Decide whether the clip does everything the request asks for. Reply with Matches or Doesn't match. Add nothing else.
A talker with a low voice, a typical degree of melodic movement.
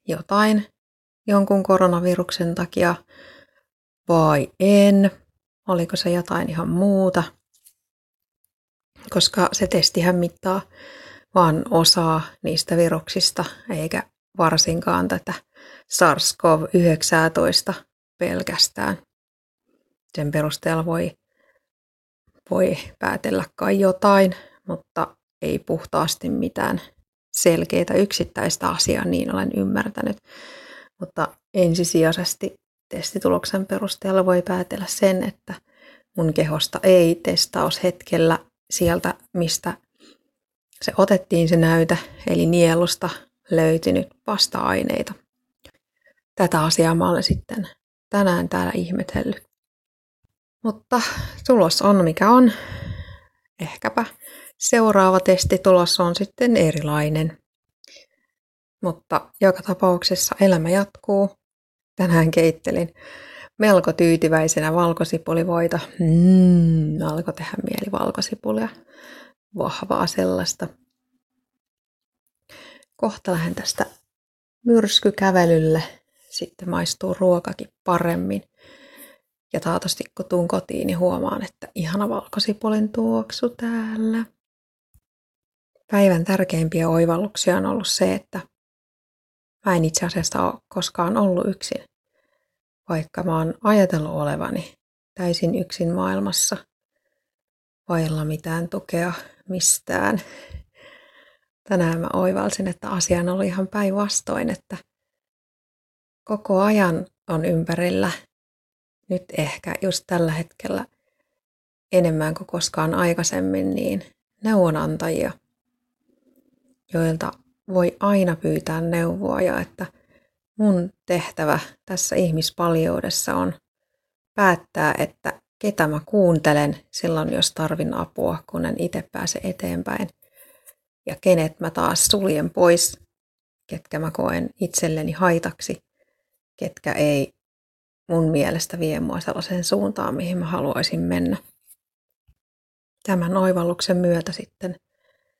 Doesn't match